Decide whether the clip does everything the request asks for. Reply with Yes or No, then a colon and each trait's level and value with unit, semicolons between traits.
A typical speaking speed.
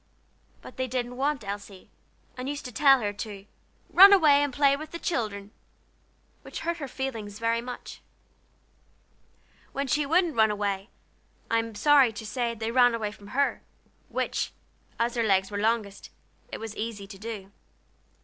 Yes: average, 165 wpm